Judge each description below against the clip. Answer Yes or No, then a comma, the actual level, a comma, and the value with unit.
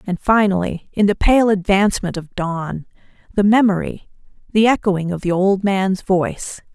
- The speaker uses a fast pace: No, average, 150 wpm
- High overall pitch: Yes, high, 195 Hz